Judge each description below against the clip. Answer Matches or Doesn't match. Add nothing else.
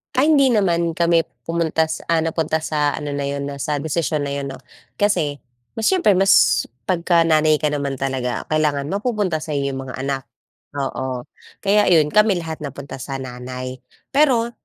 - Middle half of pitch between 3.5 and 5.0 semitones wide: Matches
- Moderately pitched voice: Matches